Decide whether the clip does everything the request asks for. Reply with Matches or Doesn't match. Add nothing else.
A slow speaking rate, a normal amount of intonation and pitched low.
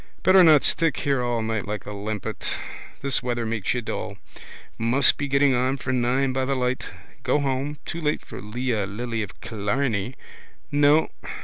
Doesn't match